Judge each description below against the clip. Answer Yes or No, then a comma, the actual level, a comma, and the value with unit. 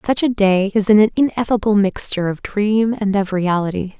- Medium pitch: No, high, 205 Hz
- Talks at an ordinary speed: Yes, average, 180 wpm